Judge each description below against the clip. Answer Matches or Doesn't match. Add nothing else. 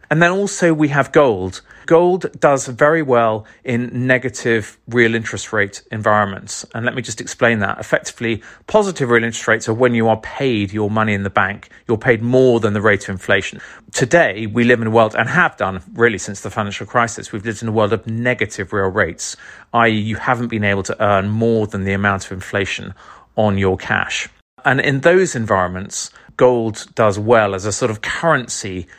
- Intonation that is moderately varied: Matches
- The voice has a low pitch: Matches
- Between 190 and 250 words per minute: Matches